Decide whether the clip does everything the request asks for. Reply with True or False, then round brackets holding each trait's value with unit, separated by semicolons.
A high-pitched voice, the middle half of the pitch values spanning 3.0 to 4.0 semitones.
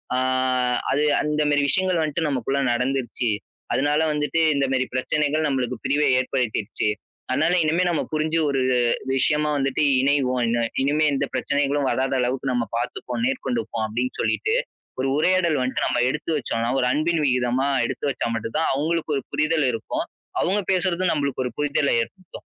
False (140 Hz; 3.4 semitones)